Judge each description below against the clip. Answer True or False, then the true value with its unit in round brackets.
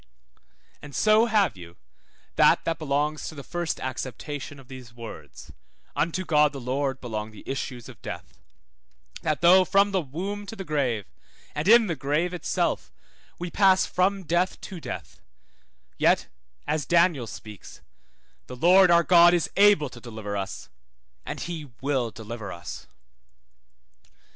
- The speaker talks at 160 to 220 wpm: False (150 wpm)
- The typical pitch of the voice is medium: True (150 Hz)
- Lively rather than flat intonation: True (6.1 semitones)